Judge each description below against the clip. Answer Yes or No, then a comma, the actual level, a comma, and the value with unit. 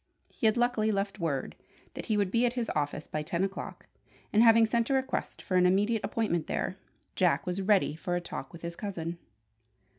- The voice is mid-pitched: No, high, 195 Hz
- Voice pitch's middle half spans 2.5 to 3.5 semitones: No, average, 4.7 semitones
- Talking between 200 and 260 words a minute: Yes, fast, 205 wpm